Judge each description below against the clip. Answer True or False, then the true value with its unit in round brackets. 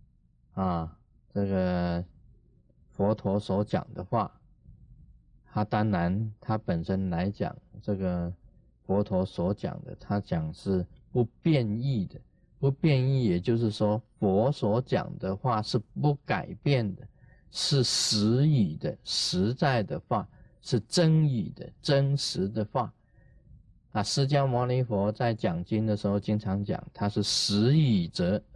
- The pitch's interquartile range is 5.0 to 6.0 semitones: True (5.3 semitones)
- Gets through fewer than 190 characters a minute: True (175 characters per minute)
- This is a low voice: True (105 Hz)